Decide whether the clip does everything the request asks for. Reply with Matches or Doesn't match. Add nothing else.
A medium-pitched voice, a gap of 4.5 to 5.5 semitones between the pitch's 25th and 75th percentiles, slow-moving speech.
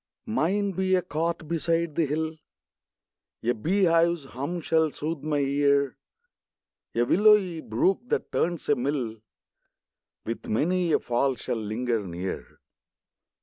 Matches